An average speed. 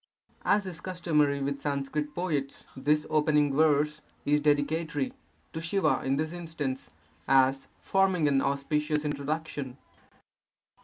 No: slow, 115 wpm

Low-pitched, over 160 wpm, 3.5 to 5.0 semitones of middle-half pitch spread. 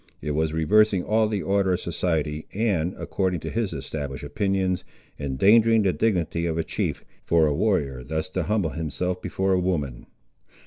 Yes: very low, 90 Hz; average, 170 wpm; average, 4.0 semitones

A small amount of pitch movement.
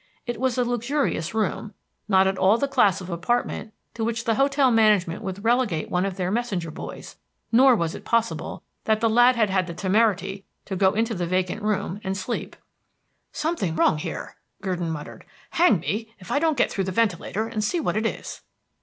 No: average, 4.0 semitones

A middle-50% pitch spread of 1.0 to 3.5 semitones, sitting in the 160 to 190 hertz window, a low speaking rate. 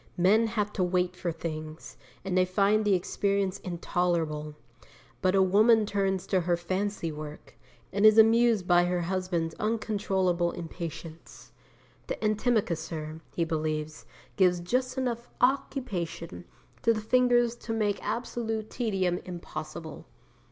No: average, 4.1 semitones; medium, 185 Hz; slow, 130 wpm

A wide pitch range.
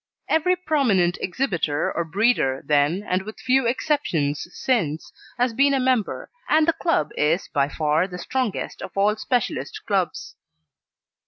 Yes: wide, 8.3 semitones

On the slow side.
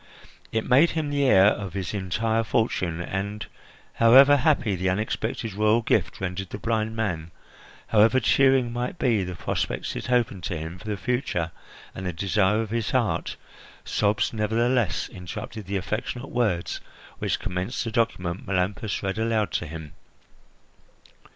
No: average, 150 wpm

